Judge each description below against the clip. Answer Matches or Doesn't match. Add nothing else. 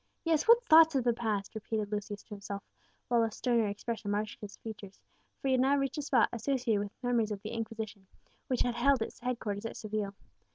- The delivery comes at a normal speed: Doesn't match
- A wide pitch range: Doesn't match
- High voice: Matches